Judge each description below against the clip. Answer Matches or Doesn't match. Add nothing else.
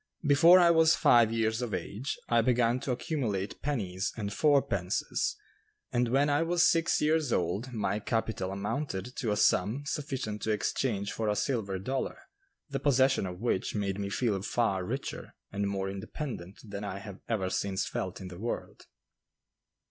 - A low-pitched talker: Matches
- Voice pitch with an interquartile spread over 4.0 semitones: Matches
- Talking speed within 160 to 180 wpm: Matches